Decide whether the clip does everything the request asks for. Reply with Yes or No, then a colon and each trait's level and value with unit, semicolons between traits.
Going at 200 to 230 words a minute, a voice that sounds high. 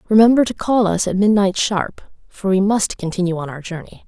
Yes: fast, 205 wpm; high, 195 Hz